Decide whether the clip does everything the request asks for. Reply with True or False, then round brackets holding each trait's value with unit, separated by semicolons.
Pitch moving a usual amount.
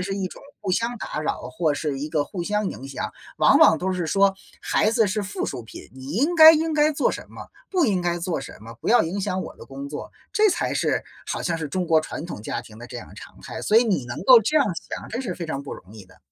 False (7.1 semitones)